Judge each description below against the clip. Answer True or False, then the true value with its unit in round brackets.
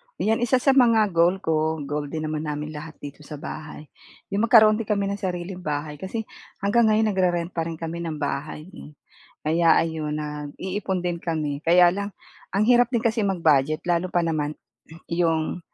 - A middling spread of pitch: True (4.6 semitones)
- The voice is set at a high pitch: False (170 Hz)